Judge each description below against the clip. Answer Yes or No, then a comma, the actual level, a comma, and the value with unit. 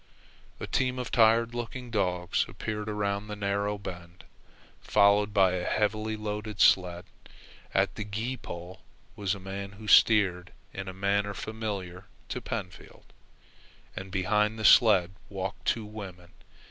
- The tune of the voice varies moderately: No, narrow, 2.3 semitones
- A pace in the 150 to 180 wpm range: No, average, 140 wpm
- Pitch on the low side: Yes, low, 100 Hz